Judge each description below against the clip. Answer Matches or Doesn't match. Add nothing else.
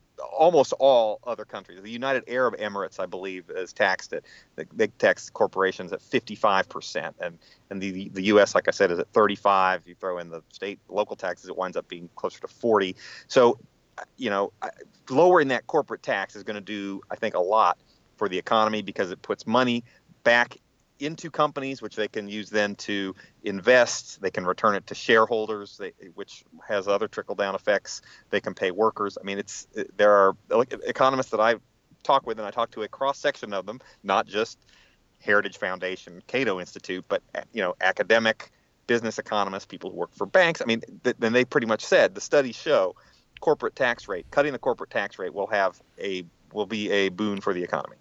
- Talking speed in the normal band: Matches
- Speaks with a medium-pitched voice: Doesn't match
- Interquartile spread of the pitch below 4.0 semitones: Matches